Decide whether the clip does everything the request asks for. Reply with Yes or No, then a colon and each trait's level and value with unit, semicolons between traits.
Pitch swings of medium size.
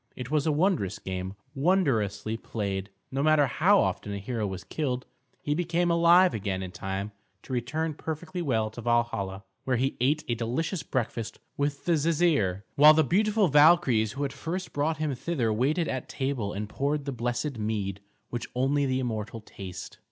No: wide, 6.2 semitones